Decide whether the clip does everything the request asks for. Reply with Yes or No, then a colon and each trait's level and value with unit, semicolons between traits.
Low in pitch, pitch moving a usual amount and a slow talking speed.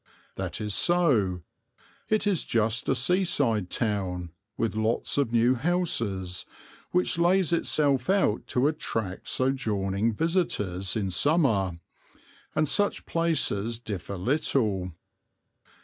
No: low, 115 Hz; wide, 8.2 semitones; slow, 110 wpm